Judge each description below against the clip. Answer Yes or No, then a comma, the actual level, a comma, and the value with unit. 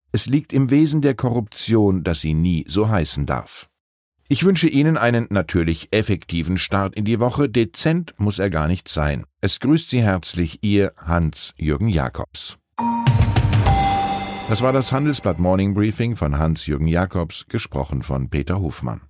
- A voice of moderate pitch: No, low, 100 Hz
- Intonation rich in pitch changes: Yes, wide, 6.6 semitones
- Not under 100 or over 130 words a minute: No, average, 150 wpm